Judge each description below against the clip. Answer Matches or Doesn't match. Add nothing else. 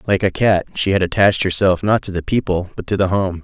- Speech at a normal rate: Doesn't match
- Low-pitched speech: Matches